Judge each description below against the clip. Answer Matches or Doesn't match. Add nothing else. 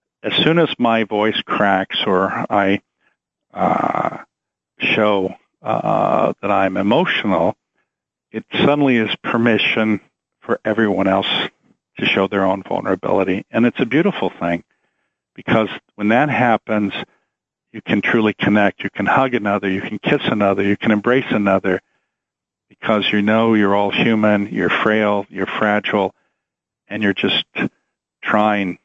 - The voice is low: Matches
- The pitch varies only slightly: Matches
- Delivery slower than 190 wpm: Matches